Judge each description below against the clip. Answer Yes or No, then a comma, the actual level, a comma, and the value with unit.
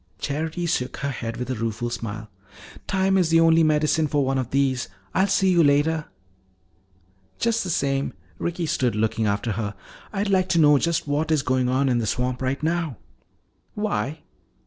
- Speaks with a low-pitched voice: No, medium, 145 Hz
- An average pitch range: Yes, average, 4.8 semitones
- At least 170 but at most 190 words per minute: Yes, average, 180 wpm